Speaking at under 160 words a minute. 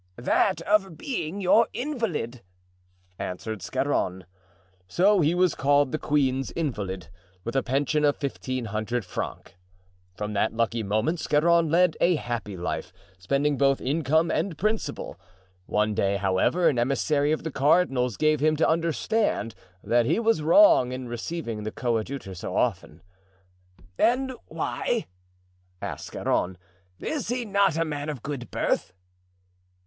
Yes: average, 140 wpm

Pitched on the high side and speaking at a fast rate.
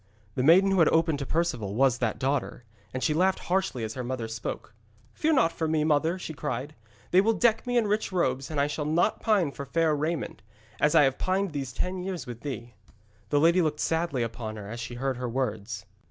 No: medium, 150 Hz; fast, 225 wpm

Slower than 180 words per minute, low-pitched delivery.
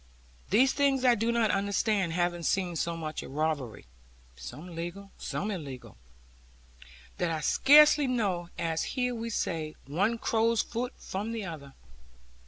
No: average, 145 wpm; high, 190 Hz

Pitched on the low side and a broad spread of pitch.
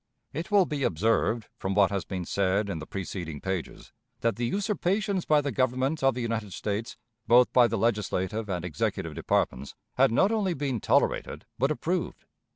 Yes: low, 115 Hz; wide, 7.0 semitones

